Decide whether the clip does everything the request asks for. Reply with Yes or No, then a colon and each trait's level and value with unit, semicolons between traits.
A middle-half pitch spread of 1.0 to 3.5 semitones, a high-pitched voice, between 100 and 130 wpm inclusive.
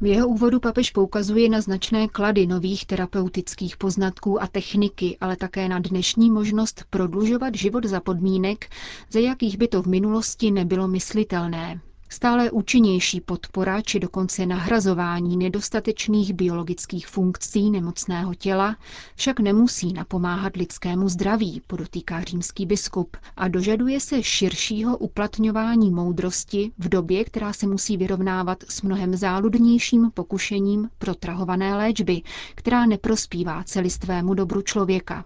Yes: average, 2.8 semitones; high, 195 Hz; average, 125 wpm